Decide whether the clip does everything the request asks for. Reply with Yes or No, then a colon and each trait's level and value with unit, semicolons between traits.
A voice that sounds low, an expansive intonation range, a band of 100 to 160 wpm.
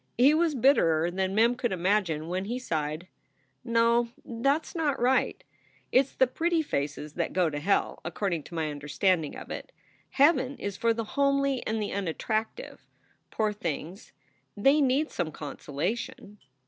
No: high, 215 Hz; wide, 7.5 semitones; average, 155 wpm